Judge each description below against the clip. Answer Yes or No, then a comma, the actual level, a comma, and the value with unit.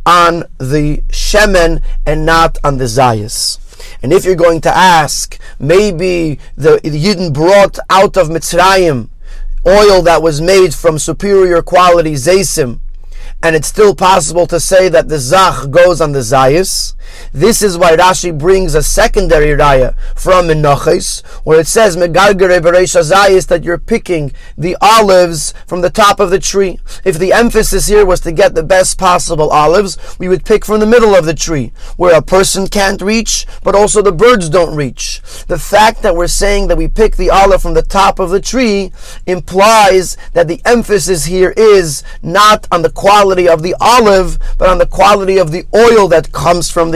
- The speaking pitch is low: No, medium, 180 Hz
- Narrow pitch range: No, average, 3.2 semitones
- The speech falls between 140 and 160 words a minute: No, average, 175 wpm